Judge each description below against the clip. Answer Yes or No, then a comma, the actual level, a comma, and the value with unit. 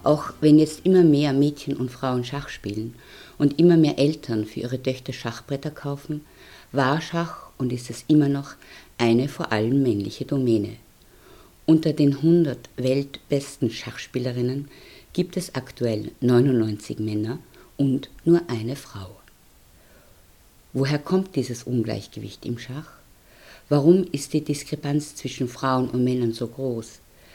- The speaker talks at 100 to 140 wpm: Yes, average, 135 wpm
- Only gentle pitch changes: No, average, 3.7 semitones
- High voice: No, low, 135 Hz